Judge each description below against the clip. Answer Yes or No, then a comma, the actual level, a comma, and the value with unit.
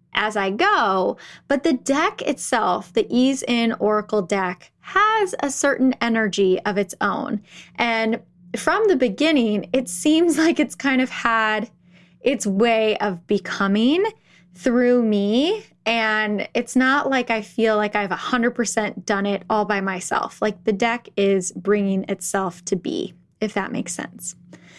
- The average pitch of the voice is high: Yes, high, 220 Hz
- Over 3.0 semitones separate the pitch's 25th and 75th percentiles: Yes, average, 4.5 semitones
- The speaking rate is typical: Yes, average, 150 wpm